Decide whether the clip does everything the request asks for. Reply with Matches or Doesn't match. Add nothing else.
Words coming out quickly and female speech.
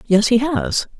Doesn't match